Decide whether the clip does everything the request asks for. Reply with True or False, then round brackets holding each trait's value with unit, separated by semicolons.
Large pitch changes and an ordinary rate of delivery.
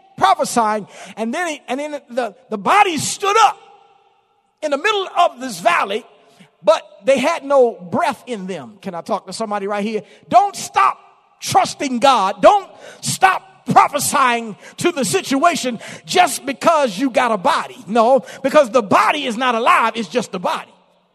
True (7.4 semitones; 165 wpm)